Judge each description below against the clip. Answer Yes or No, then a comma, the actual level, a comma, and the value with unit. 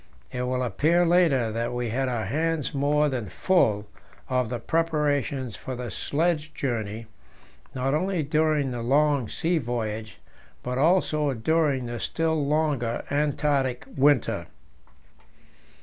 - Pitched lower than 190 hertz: Yes, low, 135 Hz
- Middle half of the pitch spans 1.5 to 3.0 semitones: No, average, 4.1 semitones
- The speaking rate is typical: No, slow, 130 wpm